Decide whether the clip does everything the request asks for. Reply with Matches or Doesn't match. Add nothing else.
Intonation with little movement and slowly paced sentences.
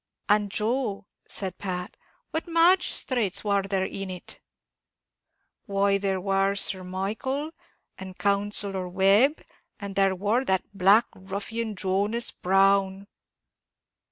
Matches